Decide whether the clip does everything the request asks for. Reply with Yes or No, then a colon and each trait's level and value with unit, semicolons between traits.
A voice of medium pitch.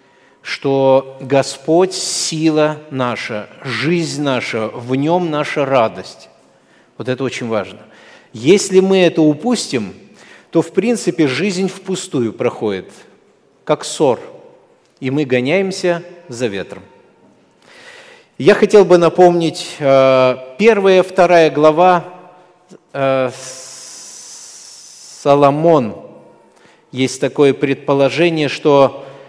Yes: medium, 155 Hz